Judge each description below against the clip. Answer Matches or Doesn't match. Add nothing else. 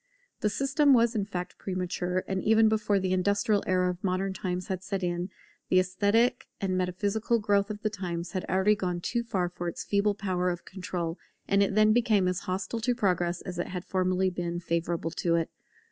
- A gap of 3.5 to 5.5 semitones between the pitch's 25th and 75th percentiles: Doesn't match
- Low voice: Doesn't match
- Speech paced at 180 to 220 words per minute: Matches